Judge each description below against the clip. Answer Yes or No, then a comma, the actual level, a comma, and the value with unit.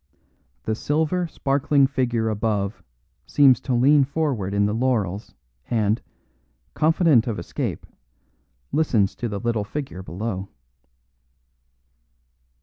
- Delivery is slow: Yes, slow, 105 wpm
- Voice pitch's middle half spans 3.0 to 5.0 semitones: No, wide, 5.4 semitones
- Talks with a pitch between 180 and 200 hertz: No, low, 120 Hz